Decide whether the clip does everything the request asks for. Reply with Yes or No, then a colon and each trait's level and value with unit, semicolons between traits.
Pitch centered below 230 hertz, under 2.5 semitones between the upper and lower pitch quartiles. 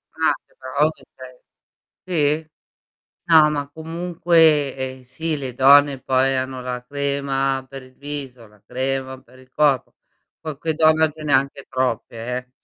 No: medium, 140 Hz; average, 2.9 semitones